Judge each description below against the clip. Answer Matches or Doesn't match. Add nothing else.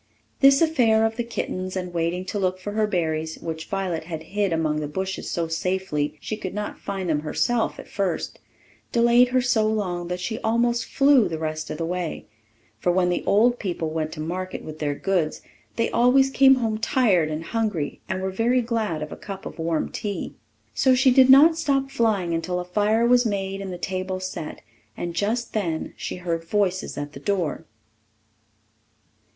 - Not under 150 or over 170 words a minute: Doesn't match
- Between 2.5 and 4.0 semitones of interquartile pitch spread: Doesn't match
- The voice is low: Doesn't match